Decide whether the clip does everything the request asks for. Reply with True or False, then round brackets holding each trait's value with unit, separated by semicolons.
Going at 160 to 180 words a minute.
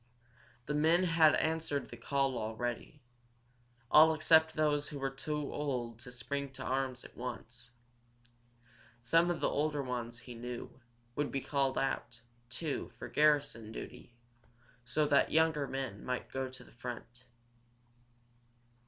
False (140 wpm)